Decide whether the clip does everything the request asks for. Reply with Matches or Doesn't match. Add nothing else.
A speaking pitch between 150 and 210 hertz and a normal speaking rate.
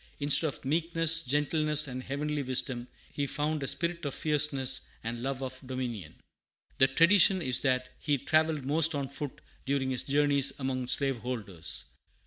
Doesn't match